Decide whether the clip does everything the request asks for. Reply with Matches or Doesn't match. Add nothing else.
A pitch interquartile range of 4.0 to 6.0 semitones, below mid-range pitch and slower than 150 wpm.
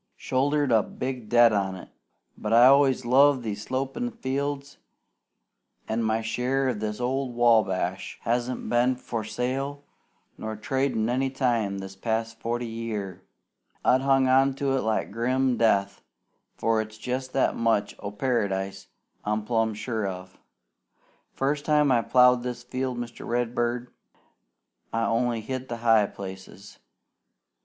Doesn't match